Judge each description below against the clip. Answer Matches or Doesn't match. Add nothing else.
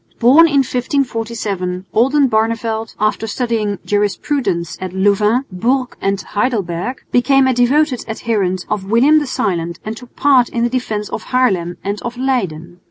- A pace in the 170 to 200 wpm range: Doesn't match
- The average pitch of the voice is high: Matches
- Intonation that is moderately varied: Matches